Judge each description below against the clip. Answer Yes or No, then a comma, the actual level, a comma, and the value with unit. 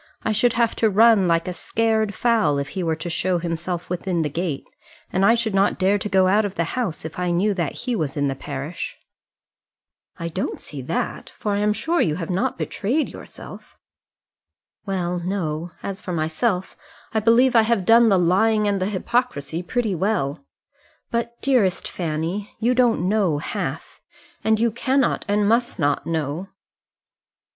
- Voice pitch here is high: Yes, high, 195 Hz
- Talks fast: No, average, 180 wpm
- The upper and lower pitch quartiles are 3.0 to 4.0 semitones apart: No, average, 4.8 semitones